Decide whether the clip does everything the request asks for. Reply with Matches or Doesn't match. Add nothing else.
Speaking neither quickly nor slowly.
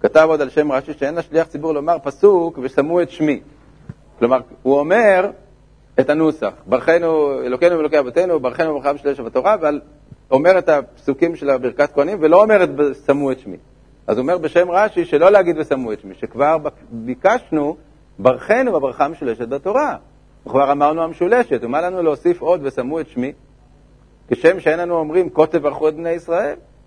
Doesn't match